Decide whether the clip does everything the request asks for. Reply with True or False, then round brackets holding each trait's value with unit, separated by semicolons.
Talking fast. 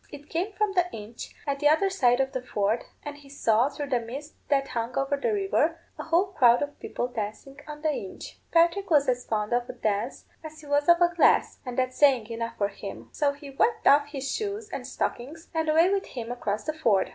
True (230 wpm)